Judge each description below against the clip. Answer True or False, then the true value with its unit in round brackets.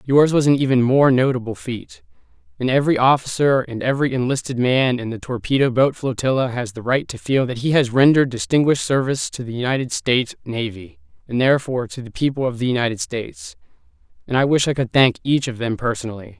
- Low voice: True (130 Hz)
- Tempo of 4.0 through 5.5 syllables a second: False (6.2 syllables/s)